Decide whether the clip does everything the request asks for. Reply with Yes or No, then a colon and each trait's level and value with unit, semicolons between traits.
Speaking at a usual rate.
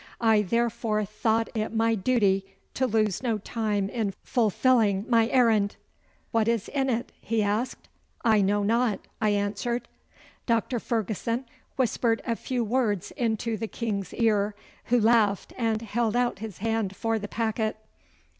Yes: average, 145 wpm